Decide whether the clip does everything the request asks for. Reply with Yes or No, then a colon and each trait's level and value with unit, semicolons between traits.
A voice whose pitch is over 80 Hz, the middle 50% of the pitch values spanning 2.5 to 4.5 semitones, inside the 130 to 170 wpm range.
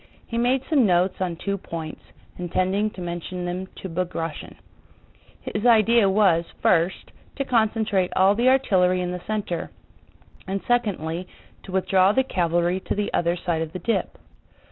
Yes: medium, 185 Hz; average, 3.5 semitones; average, 155 wpm